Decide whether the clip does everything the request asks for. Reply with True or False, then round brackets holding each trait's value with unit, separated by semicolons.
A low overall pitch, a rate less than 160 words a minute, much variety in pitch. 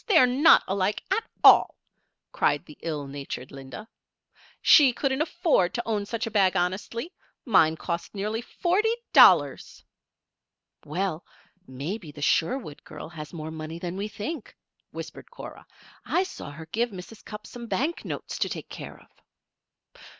False (200 Hz; 150 wpm; 7.7 semitones)